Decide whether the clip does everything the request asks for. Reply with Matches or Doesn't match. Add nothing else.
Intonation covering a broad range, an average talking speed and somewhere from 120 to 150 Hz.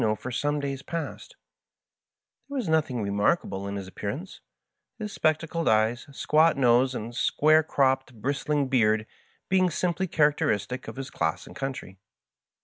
Matches